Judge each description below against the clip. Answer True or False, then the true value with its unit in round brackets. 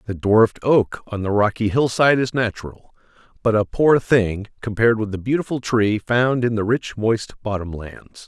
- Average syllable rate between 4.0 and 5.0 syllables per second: True (4.9 syllables/s)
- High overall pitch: False (110 Hz)